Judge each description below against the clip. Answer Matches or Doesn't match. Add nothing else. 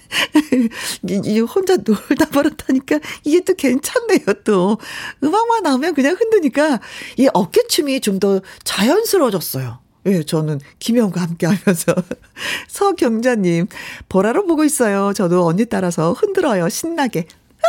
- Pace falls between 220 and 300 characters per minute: Matches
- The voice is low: Doesn't match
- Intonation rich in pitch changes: Matches